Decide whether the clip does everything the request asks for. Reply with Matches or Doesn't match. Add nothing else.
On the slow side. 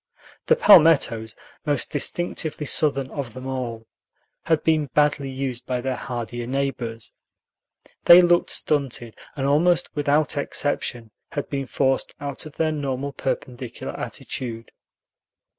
Matches